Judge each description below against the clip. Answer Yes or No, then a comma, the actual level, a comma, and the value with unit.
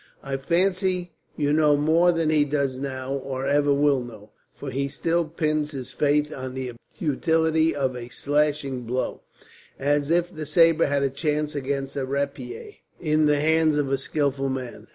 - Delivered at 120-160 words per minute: No, average, 175 wpm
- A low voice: No, medium, 145 Hz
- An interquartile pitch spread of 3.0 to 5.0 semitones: No, narrow, 2.5 semitones